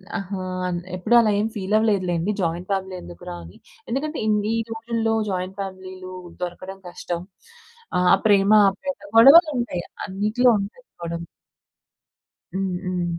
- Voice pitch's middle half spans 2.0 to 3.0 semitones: No, average, 3.7 semitones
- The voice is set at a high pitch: Yes, high, 195 Hz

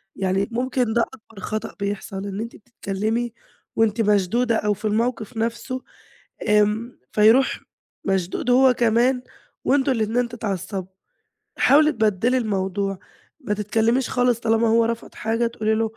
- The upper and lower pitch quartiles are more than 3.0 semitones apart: No, narrow, 2.6 semitones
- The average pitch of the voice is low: No, high, 225 Hz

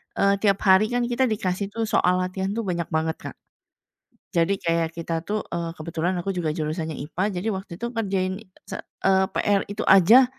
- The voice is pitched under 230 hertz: Yes, high, 190 Hz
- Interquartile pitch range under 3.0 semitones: No, average, 3.4 semitones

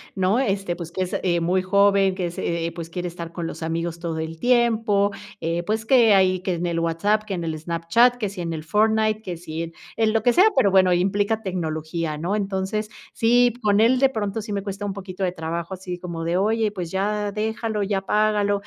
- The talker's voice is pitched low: No, high, 190 Hz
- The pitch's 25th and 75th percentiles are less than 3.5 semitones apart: No, average, 3.8 semitones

